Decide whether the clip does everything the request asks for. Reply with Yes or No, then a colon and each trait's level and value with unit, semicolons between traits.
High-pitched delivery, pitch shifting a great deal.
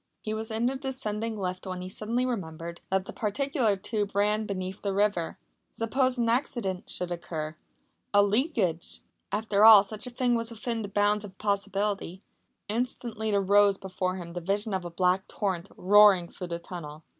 No: high, 205 Hz; average, 3.2 semitones